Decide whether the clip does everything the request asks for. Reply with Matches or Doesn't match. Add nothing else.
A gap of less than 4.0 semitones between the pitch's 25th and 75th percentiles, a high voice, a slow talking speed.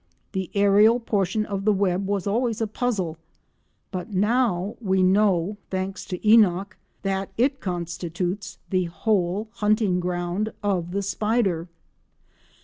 Matches